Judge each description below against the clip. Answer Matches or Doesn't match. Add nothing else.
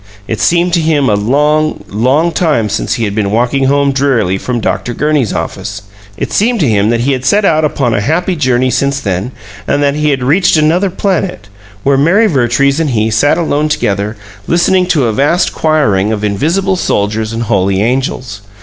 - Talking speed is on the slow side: Doesn't match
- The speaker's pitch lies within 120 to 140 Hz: Matches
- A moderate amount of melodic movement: Doesn't match